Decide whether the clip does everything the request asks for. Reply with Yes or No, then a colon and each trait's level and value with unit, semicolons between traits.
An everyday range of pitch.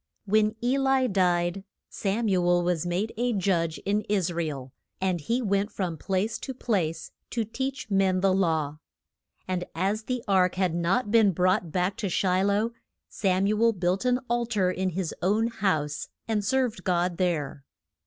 Yes: average, 3.5 semitones